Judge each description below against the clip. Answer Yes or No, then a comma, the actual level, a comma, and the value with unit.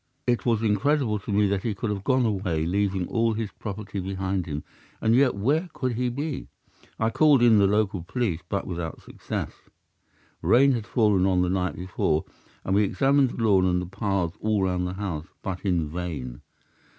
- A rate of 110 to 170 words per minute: No, average, 190 wpm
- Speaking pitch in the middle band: No, low, 100 Hz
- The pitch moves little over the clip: No, average, 4.0 semitones